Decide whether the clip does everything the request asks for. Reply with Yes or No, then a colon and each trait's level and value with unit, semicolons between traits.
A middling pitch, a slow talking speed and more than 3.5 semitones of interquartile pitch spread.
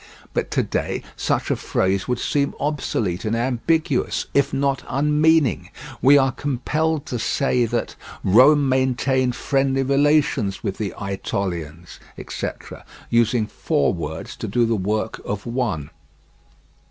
No: low, 125 Hz; slow, 130 wpm; average, 5.2 semitones